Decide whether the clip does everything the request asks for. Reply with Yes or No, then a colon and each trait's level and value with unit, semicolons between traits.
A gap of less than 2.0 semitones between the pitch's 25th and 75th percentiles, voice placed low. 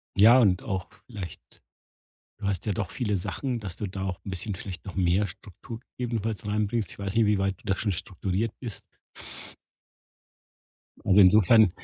No: narrow, 2.5 semitones; low, 100 Hz